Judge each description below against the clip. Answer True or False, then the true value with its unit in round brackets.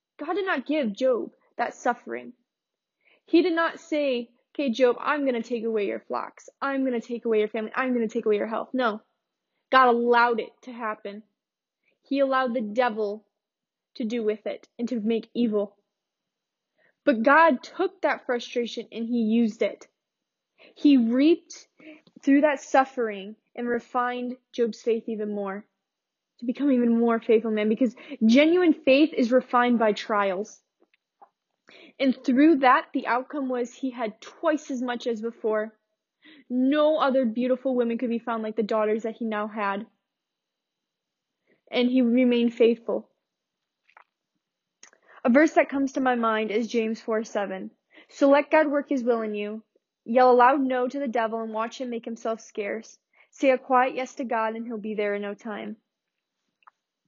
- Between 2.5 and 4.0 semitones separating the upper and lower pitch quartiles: True (3.3 semitones)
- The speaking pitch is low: False (240 Hz)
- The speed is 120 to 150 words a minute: False (170 wpm)